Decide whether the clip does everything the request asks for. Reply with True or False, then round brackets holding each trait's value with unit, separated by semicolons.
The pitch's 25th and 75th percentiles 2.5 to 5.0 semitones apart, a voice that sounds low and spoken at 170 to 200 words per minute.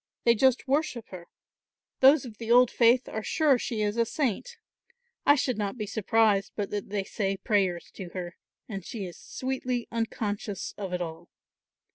False (4.1 semitones; 220 Hz; 175 wpm)